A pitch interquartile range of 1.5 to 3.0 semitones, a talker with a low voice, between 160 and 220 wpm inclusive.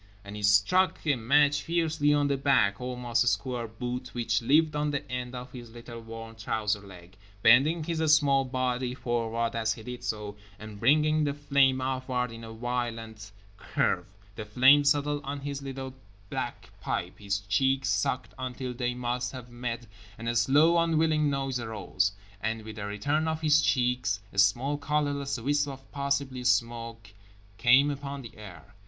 No: average, 3.8 semitones; low, 125 Hz; average, 170 wpm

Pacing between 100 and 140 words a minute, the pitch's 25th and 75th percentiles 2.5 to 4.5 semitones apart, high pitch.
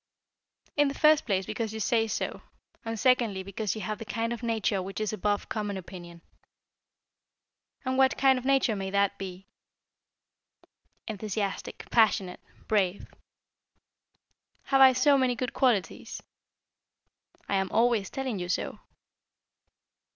Yes: slow, 135 wpm; average, 4.2 semitones; high, 220 Hz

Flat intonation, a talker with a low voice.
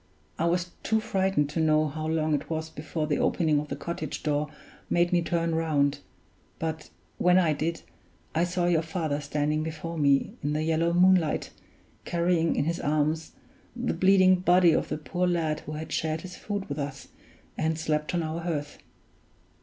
No: narrow, 2.3 semitones; medium, 160 Hz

